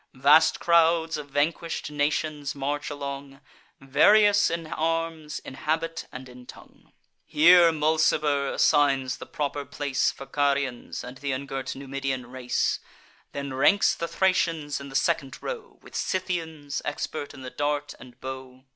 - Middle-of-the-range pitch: Yes, medium, 145 Hz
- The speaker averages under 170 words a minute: Yes, average, 140 wpm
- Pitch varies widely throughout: No, average, 3.0 semitones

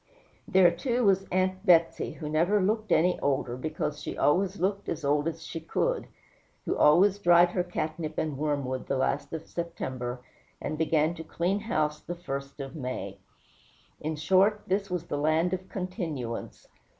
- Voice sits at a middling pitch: Yes, medium, 165 Hz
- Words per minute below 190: Yes, average, 165 wpm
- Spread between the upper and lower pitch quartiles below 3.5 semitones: No, average, 3.9 semitones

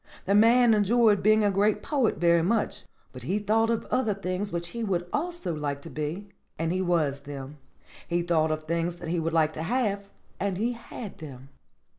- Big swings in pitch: No, average, 4.8 semitones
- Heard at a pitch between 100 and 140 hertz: No, medium, 185 Hz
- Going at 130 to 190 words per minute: No, average, 200 wpm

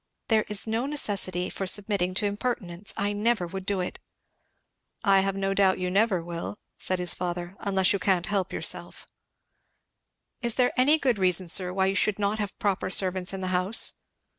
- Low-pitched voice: No, high, 195 Hz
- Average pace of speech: Yes, average, 185 wpm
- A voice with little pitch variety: Yes, narrow, 2.2 semitones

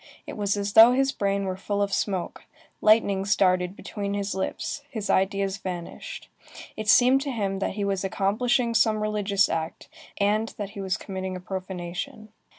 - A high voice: Yes, high, 200 Hz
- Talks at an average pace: Yes, average, 170 wpm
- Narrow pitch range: Yes, narrow, 2.0 semitones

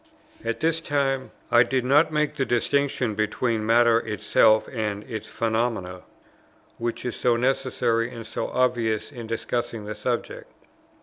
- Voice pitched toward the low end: Yes, low, 120 Hz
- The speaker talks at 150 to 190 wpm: No, average, 140 wpm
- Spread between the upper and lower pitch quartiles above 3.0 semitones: No, narrow, 2.6 semitones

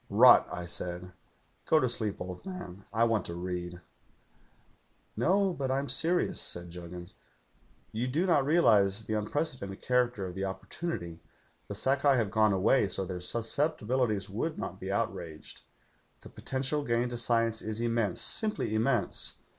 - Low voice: Yes, low, 110 Hz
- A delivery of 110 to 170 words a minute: Yes, average, 160 wpm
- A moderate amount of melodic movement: No, wide, 5.8 semitones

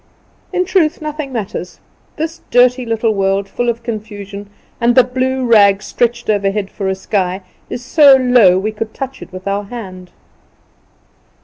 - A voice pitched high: Yes, high, 225 Hz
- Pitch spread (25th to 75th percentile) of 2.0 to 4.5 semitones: Yes, average, 4.2 semitones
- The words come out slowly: No, average, 155 wpm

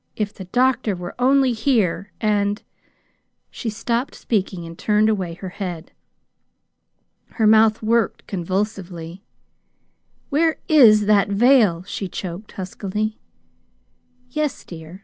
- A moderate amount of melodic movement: Yes, average, 3.8 semitones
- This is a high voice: Yes, high, 210 Hz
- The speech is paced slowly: Yes, slow, 115 wpm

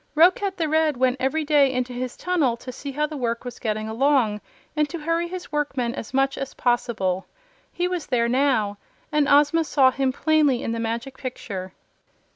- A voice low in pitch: No, very high, 270 Hz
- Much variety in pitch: No, average, 4.2 semitones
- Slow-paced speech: No, average, 190 wpm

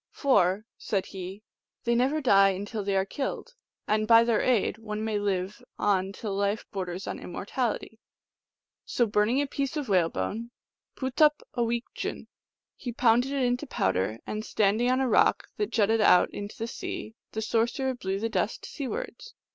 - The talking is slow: No, average, 170 wpm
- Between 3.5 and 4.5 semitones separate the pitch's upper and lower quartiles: Yes, average, 3.9 semitones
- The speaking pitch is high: Yes, high, 220 Hz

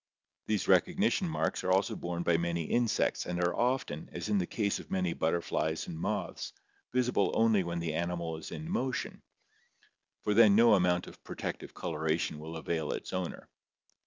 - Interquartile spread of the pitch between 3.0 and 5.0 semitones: Yes, average, 4.5 semitones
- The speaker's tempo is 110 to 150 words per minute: No, average, 170 wpm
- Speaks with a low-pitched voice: Yes, very low, 90 Hz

